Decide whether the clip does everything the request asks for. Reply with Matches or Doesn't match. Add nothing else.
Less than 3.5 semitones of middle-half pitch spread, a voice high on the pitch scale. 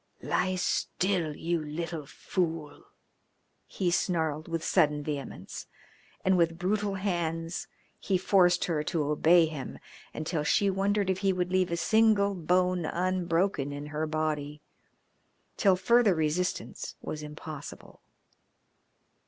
Doesn't match